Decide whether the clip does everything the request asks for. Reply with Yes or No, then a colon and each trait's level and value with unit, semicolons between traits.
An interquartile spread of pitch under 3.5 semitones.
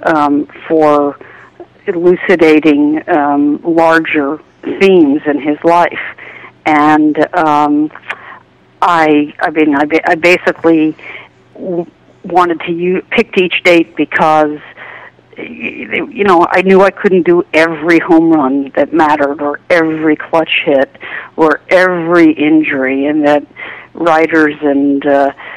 Yes: average, 2.7 semitones